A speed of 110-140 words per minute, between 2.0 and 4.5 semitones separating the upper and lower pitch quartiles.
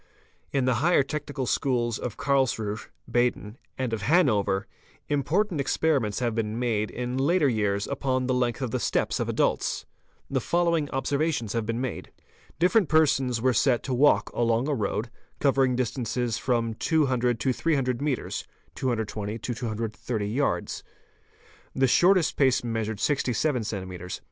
No: average, 150 wpm; average, 3.6 semitones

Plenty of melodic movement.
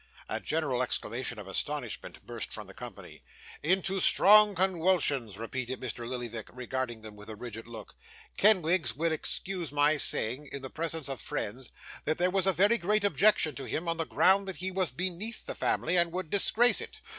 Yes: wide, 6.9 semitones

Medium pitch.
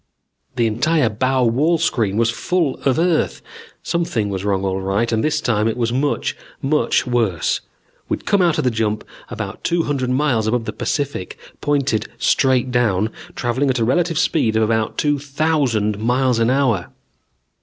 No: low, 125 Hz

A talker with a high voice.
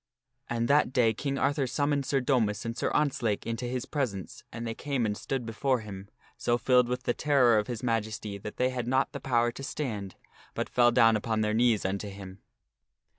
No: low, 120 Hz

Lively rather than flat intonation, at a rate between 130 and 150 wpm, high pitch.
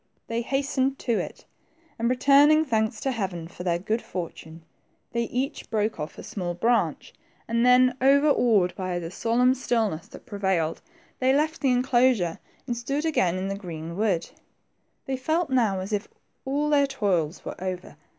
No: wide, 6.1 semitones; average, 170 wpm; high, 230 Hz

